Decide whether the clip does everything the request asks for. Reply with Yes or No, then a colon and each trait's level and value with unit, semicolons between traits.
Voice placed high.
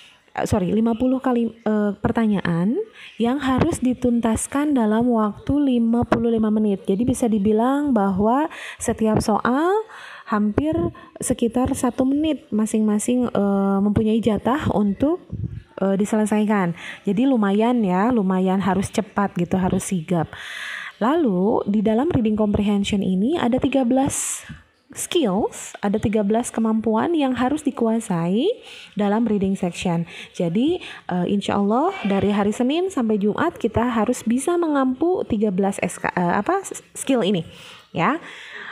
Yes: high, 225 Hz